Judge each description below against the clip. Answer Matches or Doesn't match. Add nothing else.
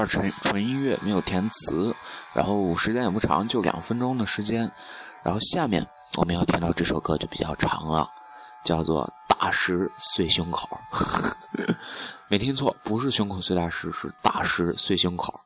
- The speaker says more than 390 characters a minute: Doesn't match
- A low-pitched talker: Matches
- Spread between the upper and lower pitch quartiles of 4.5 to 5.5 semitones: Doesn't match